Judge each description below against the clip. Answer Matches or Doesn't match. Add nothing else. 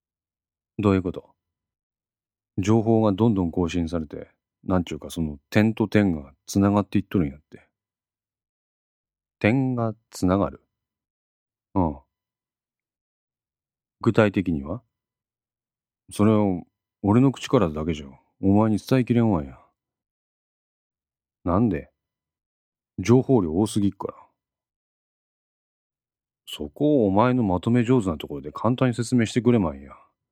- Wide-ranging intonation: Doesn't match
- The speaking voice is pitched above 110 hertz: Doesn't match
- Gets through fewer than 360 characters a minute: Matches